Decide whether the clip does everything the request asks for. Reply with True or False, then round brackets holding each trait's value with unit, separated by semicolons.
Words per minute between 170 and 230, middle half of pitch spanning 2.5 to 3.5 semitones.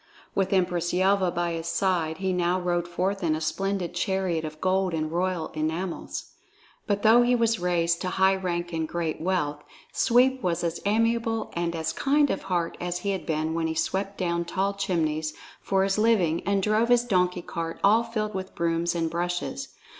True (190 wpm; 2.8 semitones)